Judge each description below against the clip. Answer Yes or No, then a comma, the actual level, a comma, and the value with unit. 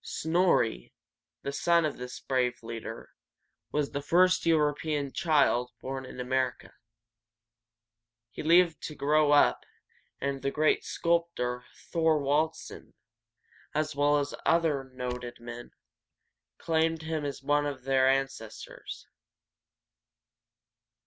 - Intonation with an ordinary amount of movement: Yes, average, 3.5 semitones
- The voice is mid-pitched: Yes, medium, 145 Hz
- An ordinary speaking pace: No, slow, 115 wpm